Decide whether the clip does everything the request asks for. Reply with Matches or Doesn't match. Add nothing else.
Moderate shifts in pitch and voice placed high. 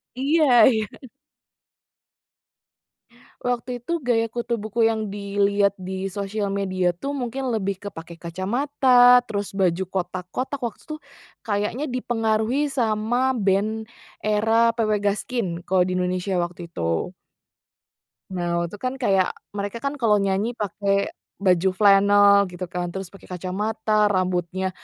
Matches